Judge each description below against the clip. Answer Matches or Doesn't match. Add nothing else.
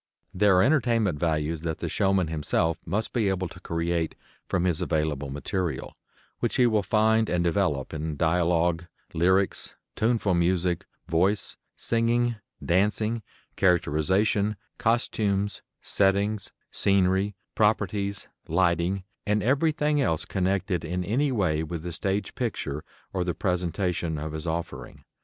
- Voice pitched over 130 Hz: Doesn't match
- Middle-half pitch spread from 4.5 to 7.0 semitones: Doesn't match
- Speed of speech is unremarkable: Doesn't match